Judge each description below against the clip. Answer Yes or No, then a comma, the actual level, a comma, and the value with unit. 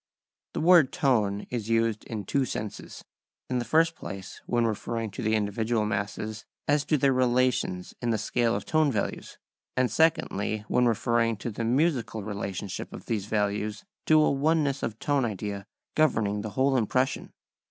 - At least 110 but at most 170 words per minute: Yes, average, 165 wpm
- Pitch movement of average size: Yes, average, 4.0 semitones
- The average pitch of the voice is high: No, low, 115 Hz